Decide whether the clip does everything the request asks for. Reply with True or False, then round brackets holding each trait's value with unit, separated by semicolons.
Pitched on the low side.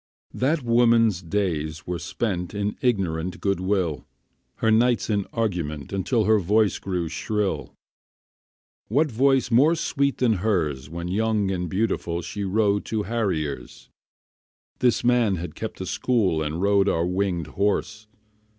True (100 Hz)